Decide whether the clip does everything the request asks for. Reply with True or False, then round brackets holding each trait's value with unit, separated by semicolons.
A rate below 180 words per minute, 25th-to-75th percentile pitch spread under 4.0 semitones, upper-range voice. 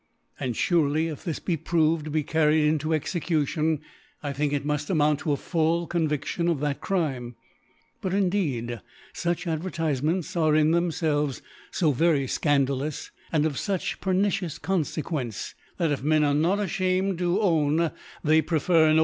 False (155 wpm; 2.7 semitones; 155 Hz)